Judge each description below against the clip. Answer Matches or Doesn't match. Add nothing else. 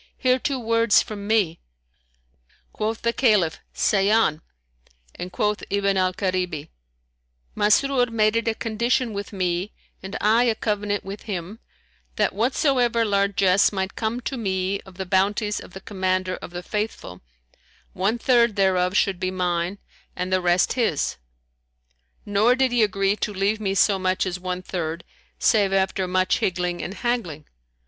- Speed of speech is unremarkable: Matches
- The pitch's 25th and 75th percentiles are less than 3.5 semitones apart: Matches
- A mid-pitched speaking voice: Doesn't match